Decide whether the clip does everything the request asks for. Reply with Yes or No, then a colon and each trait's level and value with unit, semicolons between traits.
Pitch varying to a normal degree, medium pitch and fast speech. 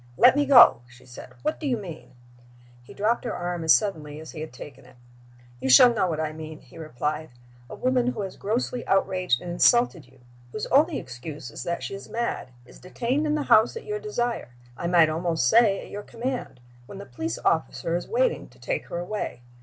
No: wide, 7.6 semitones; medium, 180 Hz; fast, 215 wpm